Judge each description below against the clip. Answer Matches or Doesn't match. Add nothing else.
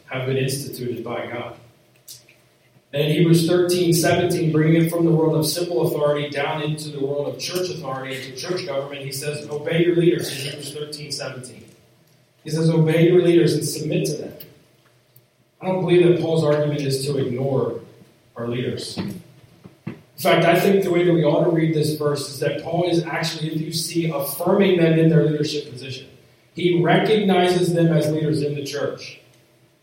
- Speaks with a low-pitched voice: Doesn't match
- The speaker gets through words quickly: Doesn't match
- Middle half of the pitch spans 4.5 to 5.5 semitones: Doesn't match